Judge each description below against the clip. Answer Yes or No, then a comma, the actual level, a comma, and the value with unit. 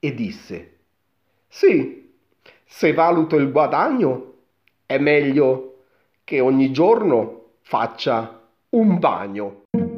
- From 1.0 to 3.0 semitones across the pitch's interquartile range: No, average, 4.8 semitones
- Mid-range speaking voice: Yes, medium, 145 Hz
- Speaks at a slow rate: Yes, slow, 90 wpm